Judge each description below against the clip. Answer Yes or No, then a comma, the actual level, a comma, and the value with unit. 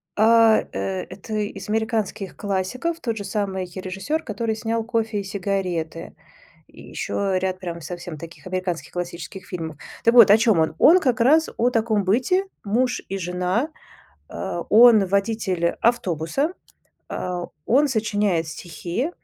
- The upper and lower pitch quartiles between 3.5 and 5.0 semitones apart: Yes, average, 4.2 semitones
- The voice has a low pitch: No, high, 200 Hz